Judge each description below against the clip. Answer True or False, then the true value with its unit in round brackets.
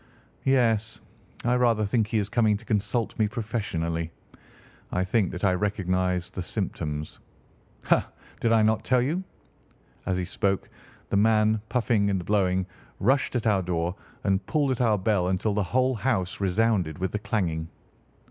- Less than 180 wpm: True (160 wpm)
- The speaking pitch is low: True (105 Hz)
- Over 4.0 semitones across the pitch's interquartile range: False (3.6 semitones)